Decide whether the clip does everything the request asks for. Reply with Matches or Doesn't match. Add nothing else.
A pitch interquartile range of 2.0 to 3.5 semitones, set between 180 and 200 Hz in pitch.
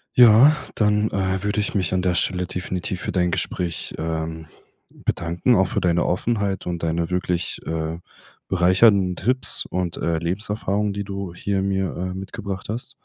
Doesn't match